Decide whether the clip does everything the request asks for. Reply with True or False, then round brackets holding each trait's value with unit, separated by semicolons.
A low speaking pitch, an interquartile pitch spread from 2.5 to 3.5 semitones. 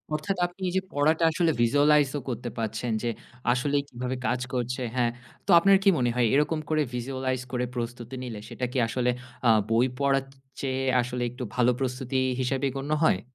True (130 Hz; 2.8 semitones)